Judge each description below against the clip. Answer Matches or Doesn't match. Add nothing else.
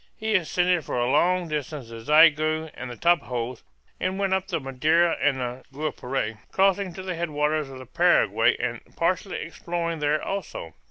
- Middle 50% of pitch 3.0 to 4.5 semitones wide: Doesn't match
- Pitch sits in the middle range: Matches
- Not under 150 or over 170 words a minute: Matches